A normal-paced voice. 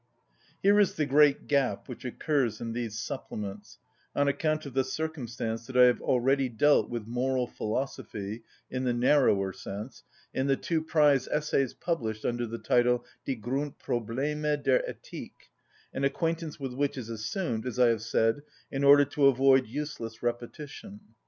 Yes: average, 160 wpm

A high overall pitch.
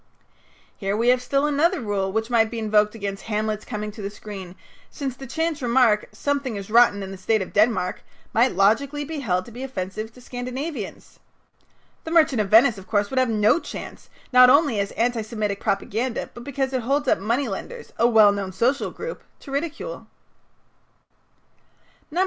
Yes: high, 230 Hz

